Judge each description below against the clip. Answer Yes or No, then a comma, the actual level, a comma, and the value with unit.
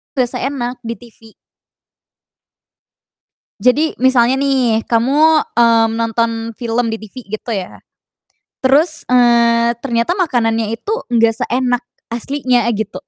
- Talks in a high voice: Yes, high, 240 Hz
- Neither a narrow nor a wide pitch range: No, narrow, 2.3 semitones